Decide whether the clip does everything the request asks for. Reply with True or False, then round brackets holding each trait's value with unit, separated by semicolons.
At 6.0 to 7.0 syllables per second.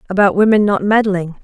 False (5.8 syllables/s)